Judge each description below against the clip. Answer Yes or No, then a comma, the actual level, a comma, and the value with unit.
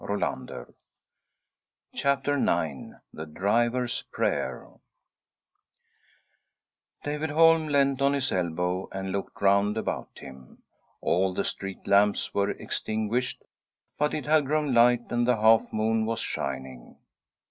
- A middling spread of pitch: No, wide, 6.3 semitones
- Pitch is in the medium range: No, low, 110 Hz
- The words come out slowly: Yes, slow, 115 wpm